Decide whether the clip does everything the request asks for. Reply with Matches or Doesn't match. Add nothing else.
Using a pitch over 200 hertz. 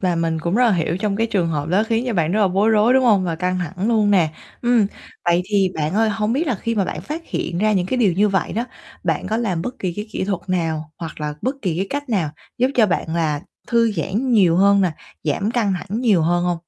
Doesn't match